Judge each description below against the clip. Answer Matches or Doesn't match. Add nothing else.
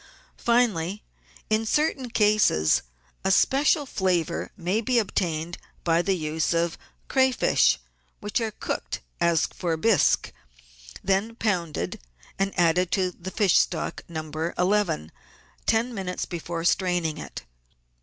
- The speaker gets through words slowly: Matches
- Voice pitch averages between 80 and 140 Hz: Doesn't match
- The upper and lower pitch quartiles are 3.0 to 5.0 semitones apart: Matches